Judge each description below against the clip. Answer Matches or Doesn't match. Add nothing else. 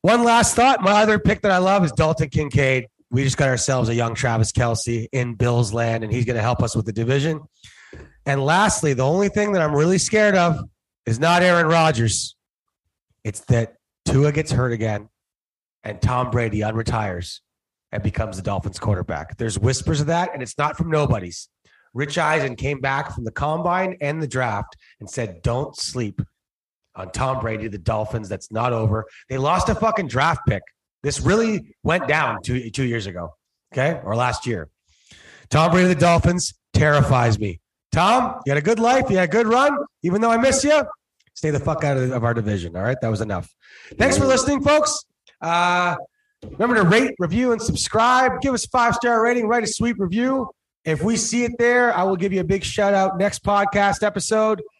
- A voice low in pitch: Doesn't match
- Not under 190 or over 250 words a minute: Matches